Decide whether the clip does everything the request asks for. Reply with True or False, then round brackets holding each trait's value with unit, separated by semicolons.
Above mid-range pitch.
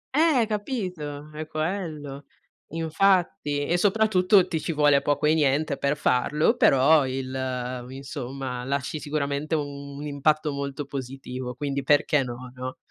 False (145 Hz)